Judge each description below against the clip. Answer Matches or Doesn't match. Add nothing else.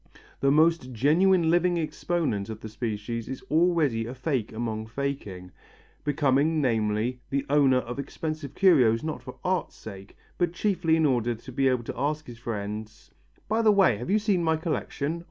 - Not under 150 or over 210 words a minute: Matches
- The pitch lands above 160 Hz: Doesn't match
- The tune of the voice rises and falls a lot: Matches